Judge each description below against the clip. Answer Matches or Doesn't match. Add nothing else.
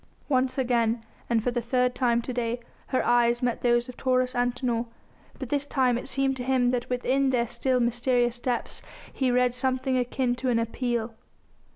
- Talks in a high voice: Matches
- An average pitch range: Doesn't match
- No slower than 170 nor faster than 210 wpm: Matches